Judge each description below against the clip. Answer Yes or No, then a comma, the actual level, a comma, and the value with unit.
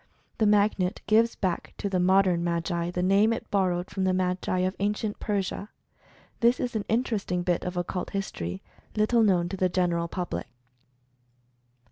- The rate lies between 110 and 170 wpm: Yes, average, 160 wpm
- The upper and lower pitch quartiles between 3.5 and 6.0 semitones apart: No, average, 2.7 semitones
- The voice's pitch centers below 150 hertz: No, medium, 185 Hz